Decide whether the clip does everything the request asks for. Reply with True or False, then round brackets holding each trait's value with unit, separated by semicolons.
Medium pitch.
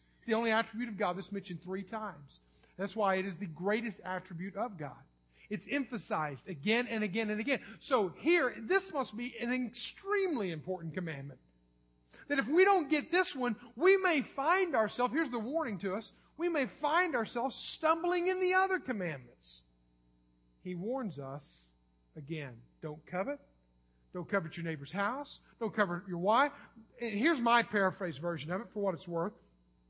False (210 Hz)